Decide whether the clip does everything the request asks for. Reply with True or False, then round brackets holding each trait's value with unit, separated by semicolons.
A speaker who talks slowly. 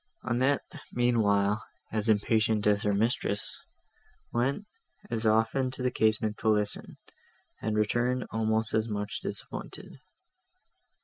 True (115 wpm)